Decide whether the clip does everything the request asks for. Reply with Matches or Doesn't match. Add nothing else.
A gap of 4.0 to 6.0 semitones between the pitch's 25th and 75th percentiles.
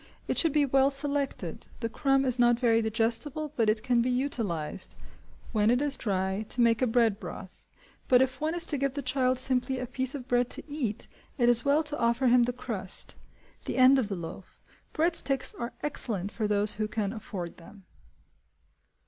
Doesn't match